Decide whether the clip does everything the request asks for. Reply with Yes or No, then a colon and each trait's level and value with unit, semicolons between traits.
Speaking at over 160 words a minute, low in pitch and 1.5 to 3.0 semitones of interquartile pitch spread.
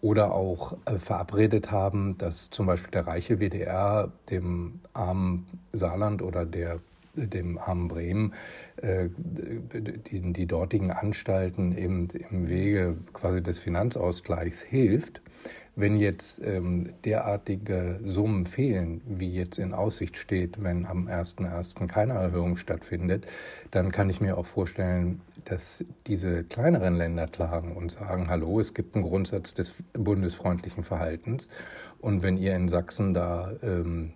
No: average, 135 wpm; very low, 90 Hz; narrow, 2.6 semitones